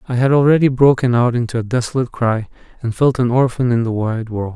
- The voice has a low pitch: Yes, low, 120 Hz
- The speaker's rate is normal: No, fast, 225 wpm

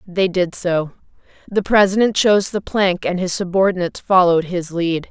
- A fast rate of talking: No, average, 165 wpm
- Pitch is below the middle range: No, medium, 185 Hz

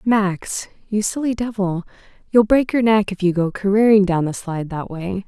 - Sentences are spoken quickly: No, average, 195 wpm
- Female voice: Yes, female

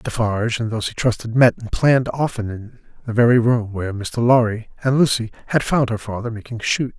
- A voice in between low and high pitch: No, low, 115 Hz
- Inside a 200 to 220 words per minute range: Yes, fast, 205 wpm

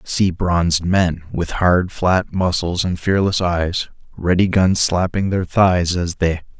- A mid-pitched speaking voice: No, very low, 90 Hz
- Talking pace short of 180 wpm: Yes, average, 155 wpm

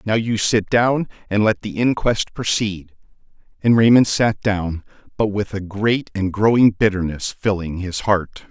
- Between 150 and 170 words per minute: Yes, average, 160 wpm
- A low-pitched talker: Yes, low, 105 Hz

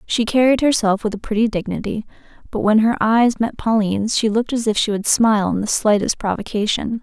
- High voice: Yes, high, 220 Hz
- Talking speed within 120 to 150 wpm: No, fast, 205 wpm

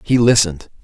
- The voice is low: Yes, low, 105 Hz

